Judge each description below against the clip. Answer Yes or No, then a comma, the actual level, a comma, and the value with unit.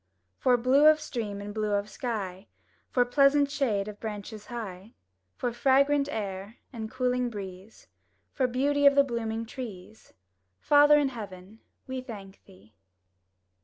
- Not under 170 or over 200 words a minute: No, average, 140 wpm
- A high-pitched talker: Yes, high, 230 Hz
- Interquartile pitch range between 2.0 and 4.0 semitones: No, average, 4.5 semitones